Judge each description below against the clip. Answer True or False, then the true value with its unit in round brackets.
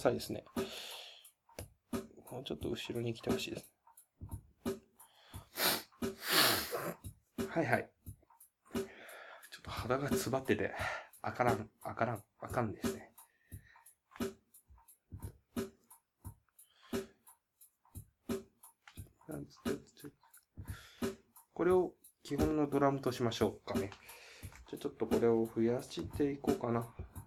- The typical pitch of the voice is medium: False (125 Hz)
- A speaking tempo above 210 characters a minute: False (185 characters per minute)